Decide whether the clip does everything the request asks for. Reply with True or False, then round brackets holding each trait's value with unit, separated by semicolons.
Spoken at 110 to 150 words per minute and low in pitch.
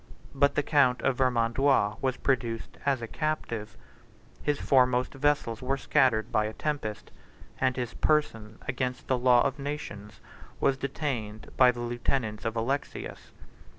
True (145 wpm; 125 Hz)